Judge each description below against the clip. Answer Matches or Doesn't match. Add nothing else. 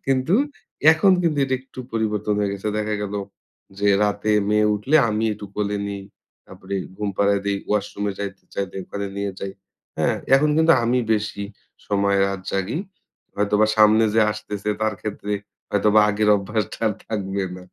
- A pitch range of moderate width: Doesn't match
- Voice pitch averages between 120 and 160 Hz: Doesn't match